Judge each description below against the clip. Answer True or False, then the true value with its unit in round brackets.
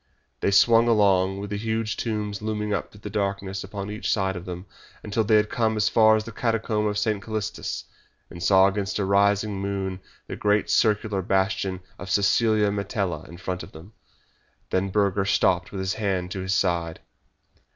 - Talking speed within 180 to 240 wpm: True (185 wpm)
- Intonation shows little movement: True (1.9 semitones)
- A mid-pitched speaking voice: False (100 Hz)